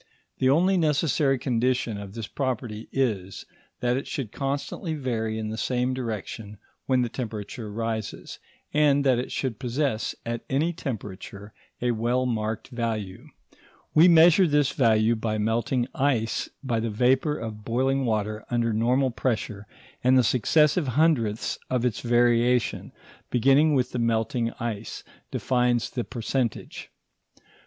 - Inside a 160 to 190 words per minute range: No, average, 140 wpm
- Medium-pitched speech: No, low, 120 Hz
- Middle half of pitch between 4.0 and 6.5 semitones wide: No, average, 3.2 semitones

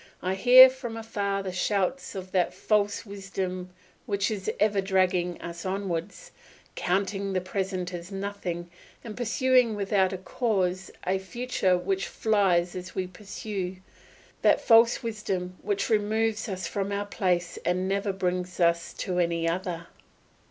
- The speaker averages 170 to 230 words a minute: No, average, 145 wpm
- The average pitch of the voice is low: No, high, 195 Hz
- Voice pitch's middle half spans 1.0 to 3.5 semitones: Yes, narrow, 2.4 semitones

